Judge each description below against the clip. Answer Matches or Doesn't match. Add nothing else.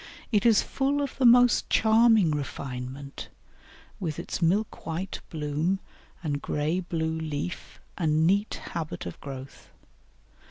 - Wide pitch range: Matches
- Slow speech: Matches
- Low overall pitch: Doesn't match